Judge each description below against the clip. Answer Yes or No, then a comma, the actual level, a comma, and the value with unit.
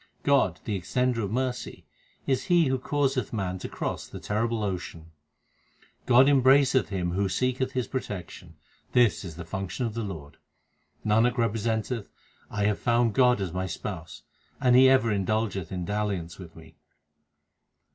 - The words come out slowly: No, average, 155 wpm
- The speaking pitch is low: Yes, low, 110 Hz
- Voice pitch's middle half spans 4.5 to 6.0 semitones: Yes, average, 5.0 semitones